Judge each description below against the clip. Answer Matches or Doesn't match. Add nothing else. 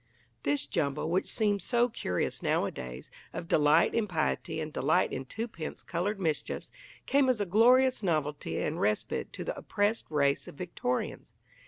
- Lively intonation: Matches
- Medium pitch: Matches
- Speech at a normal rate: Matches